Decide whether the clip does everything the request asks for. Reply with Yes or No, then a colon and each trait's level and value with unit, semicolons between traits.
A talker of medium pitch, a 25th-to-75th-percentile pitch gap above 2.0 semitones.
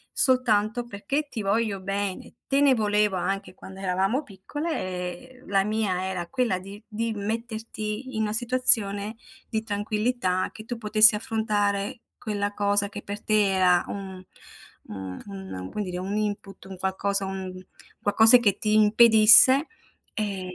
No: high, 205 Hz; narrow, 2.5 semitones